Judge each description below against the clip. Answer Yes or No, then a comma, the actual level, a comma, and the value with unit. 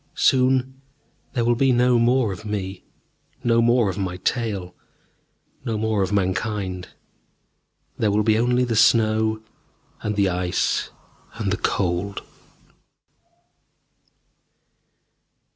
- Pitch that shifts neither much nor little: Yes, average, 3.6 semitones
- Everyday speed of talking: No, slow, 110 wpm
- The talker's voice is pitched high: No, low, 110 Hz